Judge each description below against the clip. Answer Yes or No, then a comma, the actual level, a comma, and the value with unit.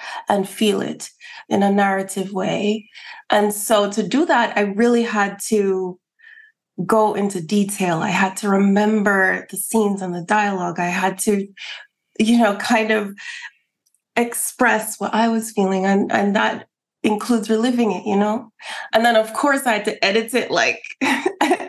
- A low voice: No, high, 210 Hz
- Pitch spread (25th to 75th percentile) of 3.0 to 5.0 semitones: No, narrow, 2.6 semitones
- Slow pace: No, average, 160 wpm